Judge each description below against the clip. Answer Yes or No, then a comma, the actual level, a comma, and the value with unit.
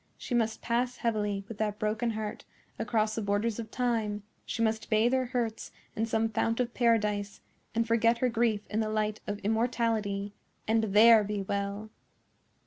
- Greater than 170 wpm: No, average, 165 wpm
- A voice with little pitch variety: Yes, narrow, 1.7 semitones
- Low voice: No, high, 220 Hz